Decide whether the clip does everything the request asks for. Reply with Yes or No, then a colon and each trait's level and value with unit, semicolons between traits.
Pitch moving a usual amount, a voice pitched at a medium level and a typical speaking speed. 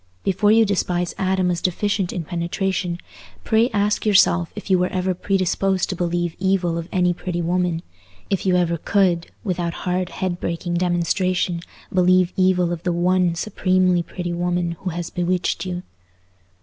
No: narrow, 1.4 semitones; medium, 180 Hz; average, 155 wpm